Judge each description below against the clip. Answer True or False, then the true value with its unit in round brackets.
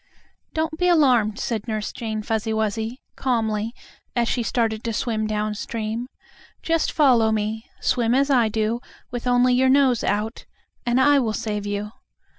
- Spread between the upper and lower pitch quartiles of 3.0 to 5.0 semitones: False (2.6 semitones)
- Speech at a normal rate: True (160 wpm)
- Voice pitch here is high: True (230 Hz)